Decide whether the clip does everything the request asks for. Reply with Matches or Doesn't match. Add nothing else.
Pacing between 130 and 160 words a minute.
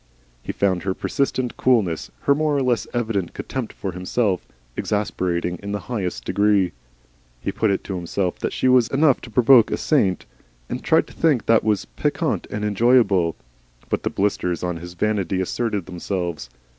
Doesn't match